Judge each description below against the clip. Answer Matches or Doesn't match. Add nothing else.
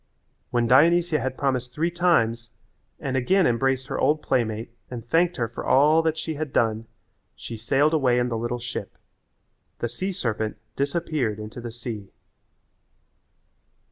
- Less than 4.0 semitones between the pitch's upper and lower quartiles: Doesn't match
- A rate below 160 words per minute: Matches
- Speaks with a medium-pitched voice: Doesn't match